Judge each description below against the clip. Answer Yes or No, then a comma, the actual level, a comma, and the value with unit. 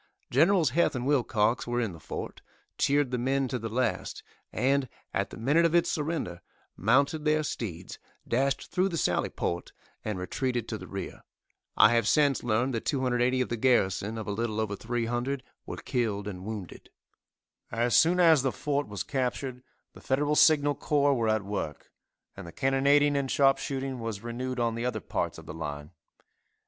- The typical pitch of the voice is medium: No, low, 125 Hz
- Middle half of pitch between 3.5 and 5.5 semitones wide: Yes, average, 4.3 semitones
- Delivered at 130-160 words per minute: No, average, 180 wpm